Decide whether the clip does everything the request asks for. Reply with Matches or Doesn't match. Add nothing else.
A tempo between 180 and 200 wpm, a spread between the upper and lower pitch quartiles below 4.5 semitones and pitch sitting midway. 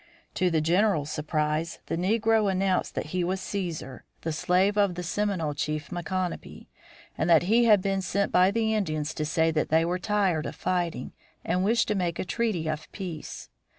Matches